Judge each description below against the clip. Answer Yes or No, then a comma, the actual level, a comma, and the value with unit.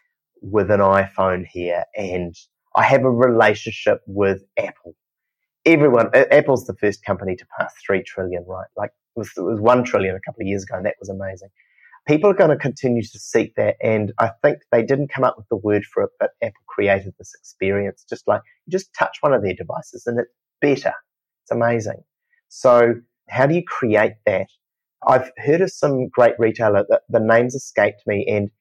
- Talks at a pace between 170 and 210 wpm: Yes, average, 200 wpm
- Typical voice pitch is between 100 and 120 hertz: Yes, low, 115 Hz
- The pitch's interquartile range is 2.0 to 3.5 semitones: No, average, 4.4 semitones